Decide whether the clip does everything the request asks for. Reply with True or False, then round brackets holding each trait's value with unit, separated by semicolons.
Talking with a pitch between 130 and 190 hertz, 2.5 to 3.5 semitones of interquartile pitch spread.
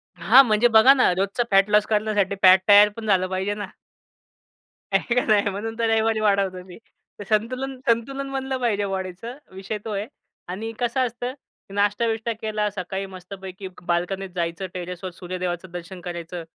False (205 Hz; 3.2 semitones)